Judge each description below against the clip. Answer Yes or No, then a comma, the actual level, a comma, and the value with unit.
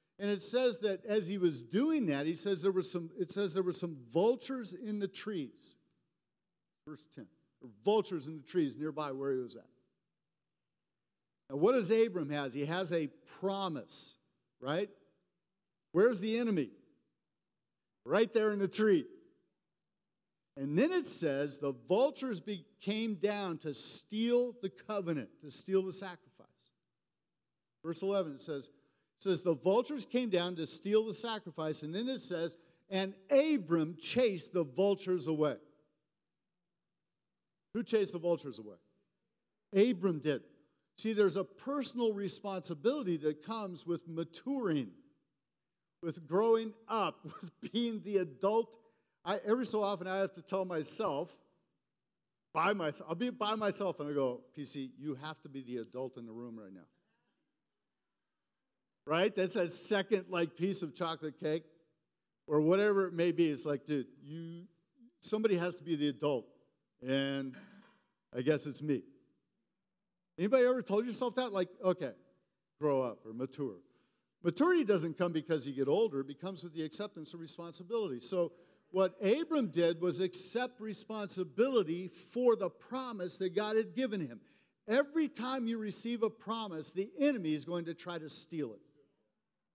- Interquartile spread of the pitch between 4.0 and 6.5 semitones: Yes, wide, 5.4 semitones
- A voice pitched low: No, medium, 180 Hz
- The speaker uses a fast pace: No, average, 155 wpm